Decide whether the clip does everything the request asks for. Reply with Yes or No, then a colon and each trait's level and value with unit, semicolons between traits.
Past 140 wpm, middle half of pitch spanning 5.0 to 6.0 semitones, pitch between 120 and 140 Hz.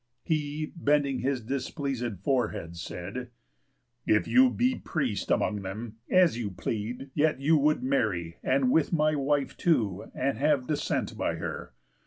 Yes: average, 150 wpm; wide, 5.4 semitones; low, 135 Hz